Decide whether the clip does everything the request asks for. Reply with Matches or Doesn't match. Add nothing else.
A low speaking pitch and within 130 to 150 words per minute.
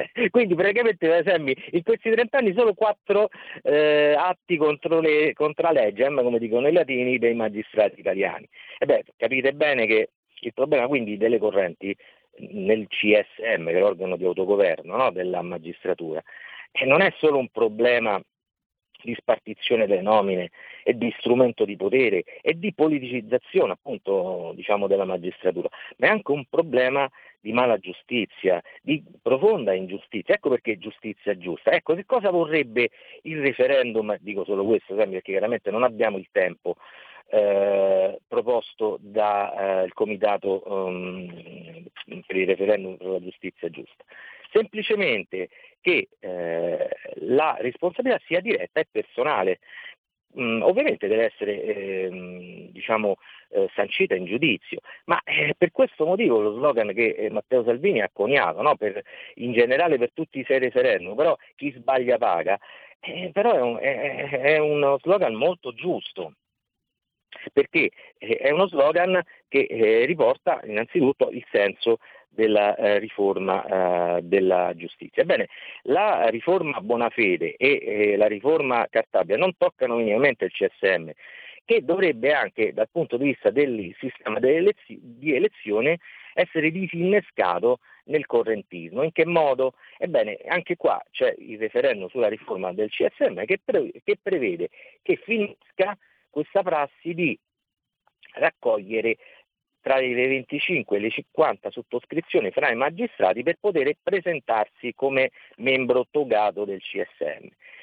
Doesn't match